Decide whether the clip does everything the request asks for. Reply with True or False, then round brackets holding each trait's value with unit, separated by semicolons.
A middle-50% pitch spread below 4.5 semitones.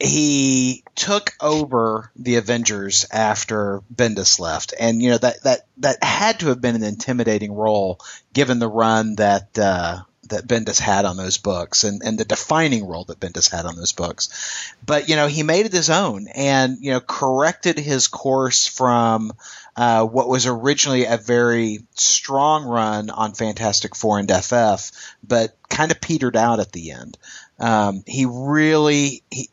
True (4.0 semitones)